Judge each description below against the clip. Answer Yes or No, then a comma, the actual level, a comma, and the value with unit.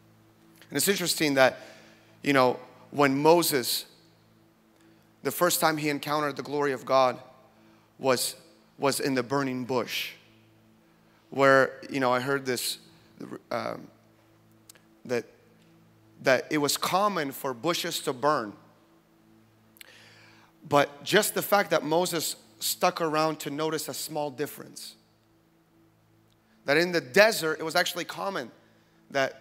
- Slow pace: Yes, slow, 125 wpm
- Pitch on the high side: No, medium, 140 Hz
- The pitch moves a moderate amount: No, wide, 6.1 semitones